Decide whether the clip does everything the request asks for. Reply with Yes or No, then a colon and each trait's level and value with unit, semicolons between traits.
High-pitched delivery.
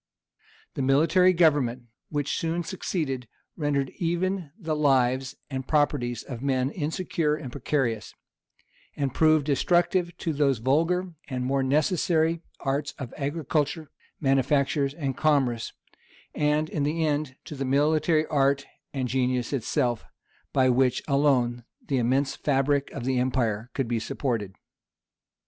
No: medium, 140 Hz